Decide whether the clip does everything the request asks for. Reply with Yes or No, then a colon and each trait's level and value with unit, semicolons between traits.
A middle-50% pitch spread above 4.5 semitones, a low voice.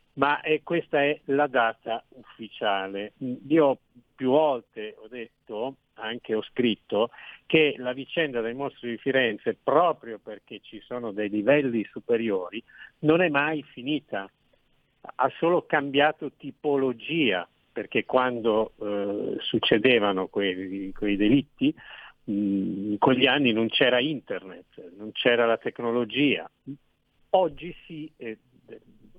Yes: average, 5.2 semitones; low, 130 Hz